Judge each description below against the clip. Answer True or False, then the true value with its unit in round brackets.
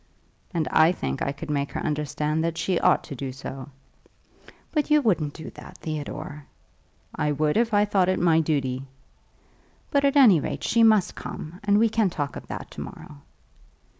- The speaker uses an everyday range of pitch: False (5.9 semitones)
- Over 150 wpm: True (185 wpm)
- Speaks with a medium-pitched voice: True (160 Hz)